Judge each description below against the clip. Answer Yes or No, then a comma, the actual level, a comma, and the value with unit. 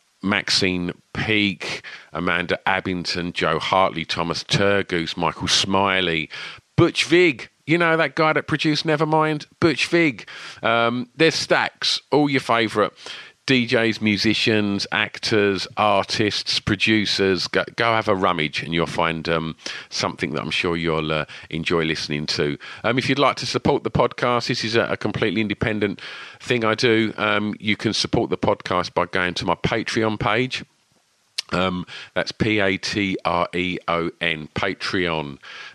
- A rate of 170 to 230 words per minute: No, average, 150 wpm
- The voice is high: No, low, 105 Hz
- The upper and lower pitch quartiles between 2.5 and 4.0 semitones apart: No, average, 4.9 semitones